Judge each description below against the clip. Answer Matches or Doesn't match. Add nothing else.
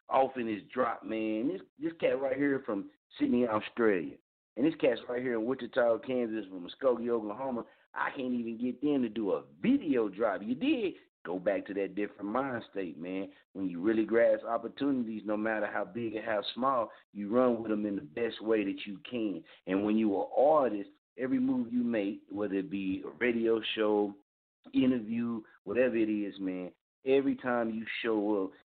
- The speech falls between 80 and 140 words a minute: Doesn't match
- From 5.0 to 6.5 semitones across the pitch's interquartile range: Doesn't match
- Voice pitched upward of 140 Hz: Doesn't match